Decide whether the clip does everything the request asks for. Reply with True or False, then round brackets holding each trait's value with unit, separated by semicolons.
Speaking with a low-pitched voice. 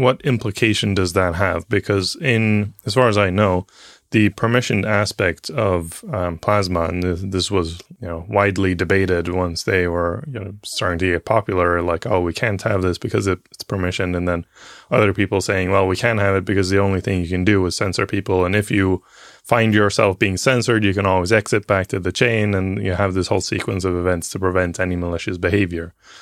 True (95 Hz)